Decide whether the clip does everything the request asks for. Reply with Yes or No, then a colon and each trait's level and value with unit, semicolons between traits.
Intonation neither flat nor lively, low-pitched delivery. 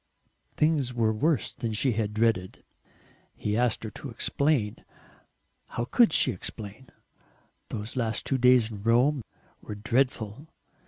Yes: average, 3.5 semitones; low, 115 Hz